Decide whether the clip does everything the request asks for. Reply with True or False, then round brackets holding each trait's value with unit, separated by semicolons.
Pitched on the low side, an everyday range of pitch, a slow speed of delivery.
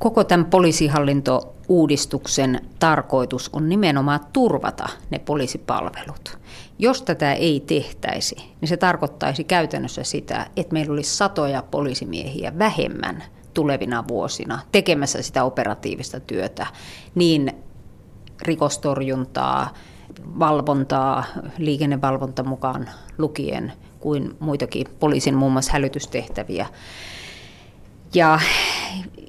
False (145 Hz; 3.5 semitones; 90 wpm)